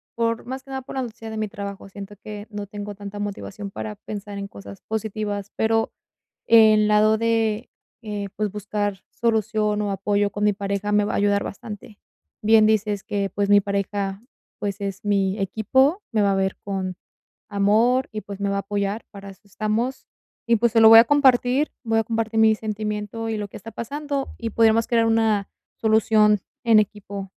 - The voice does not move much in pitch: Yes, narrow, 1.8 semitones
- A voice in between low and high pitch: No, high, 210 Hz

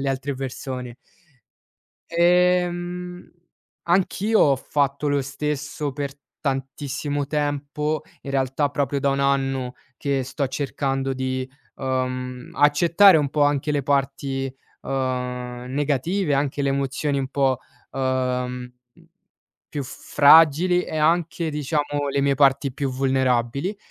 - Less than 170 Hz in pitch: Yes, medium, 140 Hz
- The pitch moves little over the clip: Yes, narrow, 2.0 semitones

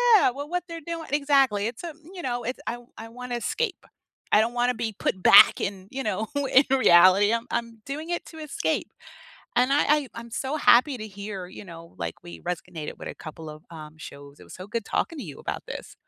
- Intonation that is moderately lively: No, wide, 6.8 semitones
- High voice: Yes, high, 230 Hz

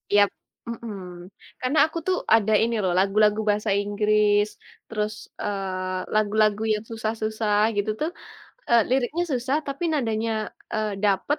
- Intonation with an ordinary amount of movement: No, narrow, 2.2 semitones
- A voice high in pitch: Yes, high, 215 Hz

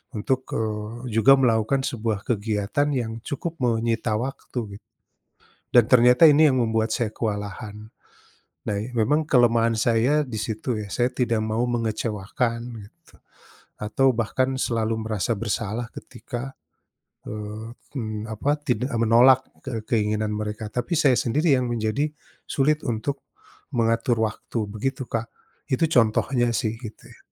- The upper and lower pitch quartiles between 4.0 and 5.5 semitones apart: No, average, 2.7 semitones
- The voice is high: No, low, 115 Hz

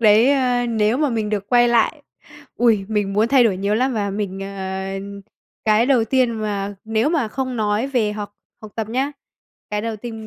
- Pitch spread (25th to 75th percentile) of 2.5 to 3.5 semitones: Yes, average, 2.8 semitones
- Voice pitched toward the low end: No, high, 220 Hz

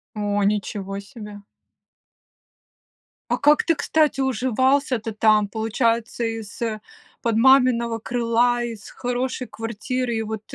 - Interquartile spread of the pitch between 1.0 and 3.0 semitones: Yes, average, 2.7 semitones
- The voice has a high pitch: Yes, high, 230 Hz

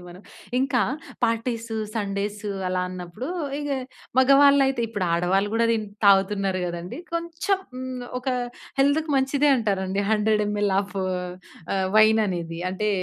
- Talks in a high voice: Yes, high, 210 Hz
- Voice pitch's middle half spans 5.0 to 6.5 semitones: Yes, wide, 5.4 semitones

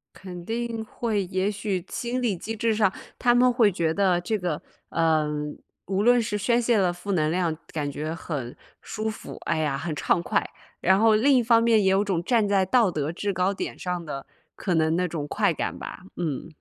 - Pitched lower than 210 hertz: Yes, high, 190 Hz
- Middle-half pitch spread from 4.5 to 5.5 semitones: Yes, average, 5.0 semitones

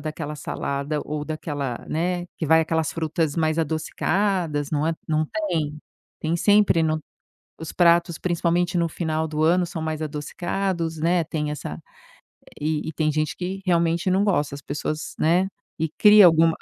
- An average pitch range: No, narrow, 2.1 semitones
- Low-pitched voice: No, medium, 160 Hz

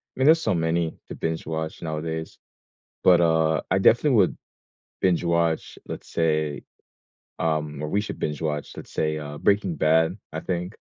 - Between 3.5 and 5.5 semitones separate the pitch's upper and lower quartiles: No, narrow, 2.4 semitones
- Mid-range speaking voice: No, very low, 80 Hz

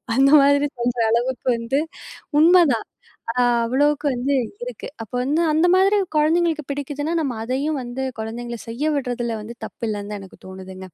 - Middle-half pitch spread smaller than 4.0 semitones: No, average, 4.3 semitones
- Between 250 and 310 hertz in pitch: Yes, very high, 260 Hz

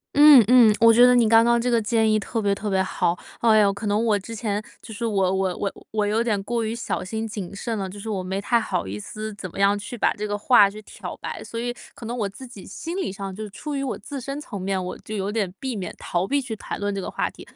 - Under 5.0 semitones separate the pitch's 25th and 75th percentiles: Yes, average, 3.0 semitones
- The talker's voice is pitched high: Yes, high, 215 Hz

